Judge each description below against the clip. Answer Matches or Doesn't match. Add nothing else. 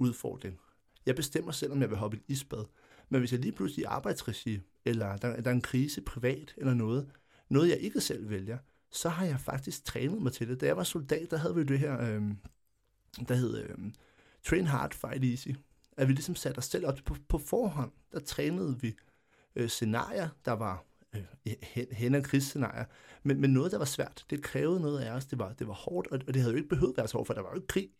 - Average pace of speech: Doesn't match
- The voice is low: Matches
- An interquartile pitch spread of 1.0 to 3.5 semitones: Matches